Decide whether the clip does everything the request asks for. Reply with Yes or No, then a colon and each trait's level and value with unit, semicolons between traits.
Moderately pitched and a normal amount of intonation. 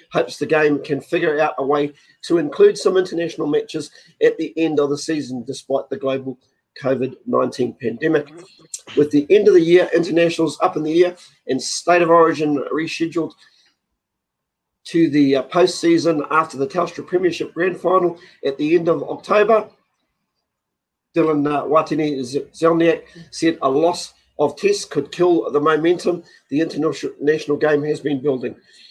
Yes: medium, 160 Hz; average, 3.1 semitones